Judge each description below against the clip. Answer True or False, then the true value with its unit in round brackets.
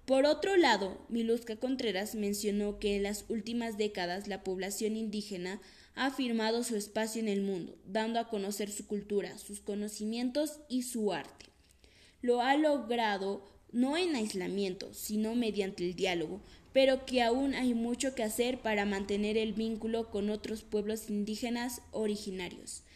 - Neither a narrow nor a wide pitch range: True (3.0 semitones)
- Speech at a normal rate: True (150 wpm)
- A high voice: True (215 Hz)